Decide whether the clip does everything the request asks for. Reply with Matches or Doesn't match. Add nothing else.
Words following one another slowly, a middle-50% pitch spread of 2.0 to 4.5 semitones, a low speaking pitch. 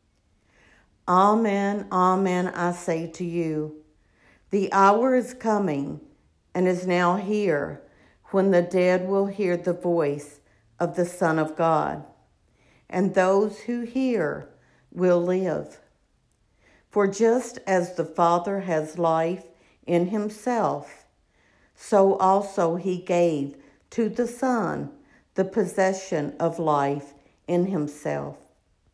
Doesn't match